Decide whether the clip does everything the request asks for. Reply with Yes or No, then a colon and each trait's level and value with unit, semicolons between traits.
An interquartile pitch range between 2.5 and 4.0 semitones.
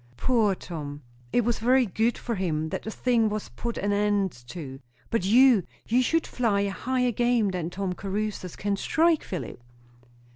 No: average, 4.4 semitones